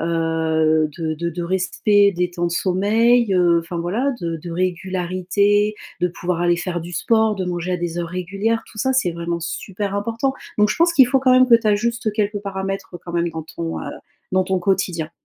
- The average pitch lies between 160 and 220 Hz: Yes, medium, 185 Hz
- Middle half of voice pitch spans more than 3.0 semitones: Yes, average, 3.5 semitones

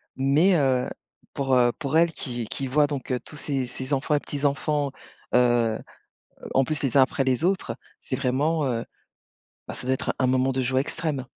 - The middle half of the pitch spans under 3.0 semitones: Yes, narrow, 2.4 semitones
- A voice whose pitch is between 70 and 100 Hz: No, low, 135 Hz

